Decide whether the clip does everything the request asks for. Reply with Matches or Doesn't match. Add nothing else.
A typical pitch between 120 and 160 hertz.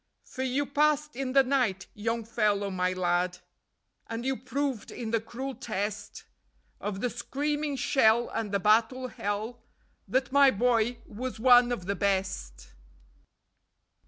Doesn't match